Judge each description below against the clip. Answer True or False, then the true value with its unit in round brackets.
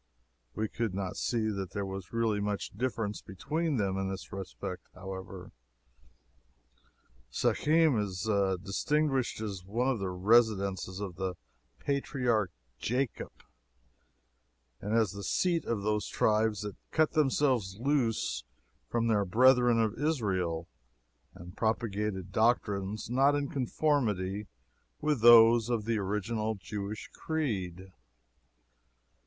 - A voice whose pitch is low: True (110 Hz)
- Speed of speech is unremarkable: False (115 wpm)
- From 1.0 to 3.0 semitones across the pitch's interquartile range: False (4.0 semitones)